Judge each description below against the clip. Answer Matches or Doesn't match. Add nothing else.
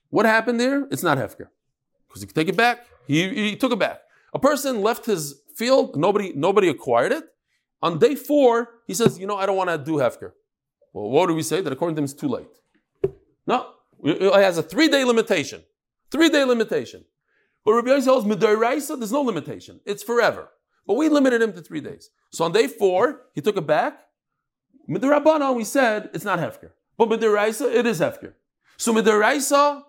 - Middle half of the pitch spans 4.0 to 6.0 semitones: Matches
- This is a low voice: Doesn't match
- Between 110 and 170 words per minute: Doesn't match